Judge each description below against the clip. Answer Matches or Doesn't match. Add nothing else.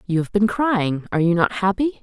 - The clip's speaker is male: Doesn't match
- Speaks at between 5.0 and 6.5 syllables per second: Matches